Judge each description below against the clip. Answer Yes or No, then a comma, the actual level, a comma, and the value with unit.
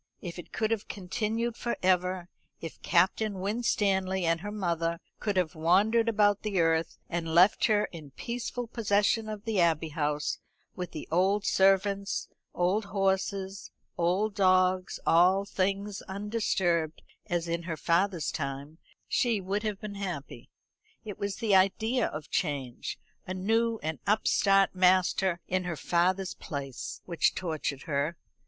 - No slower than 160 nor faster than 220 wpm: No, average, 145 wpm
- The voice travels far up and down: No, average, 3.4 semitones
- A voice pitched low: No, high, 190 Hz